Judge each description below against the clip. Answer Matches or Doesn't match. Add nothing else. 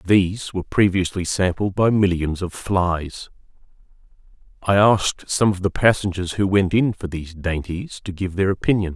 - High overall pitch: Doesn't match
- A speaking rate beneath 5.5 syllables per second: Matches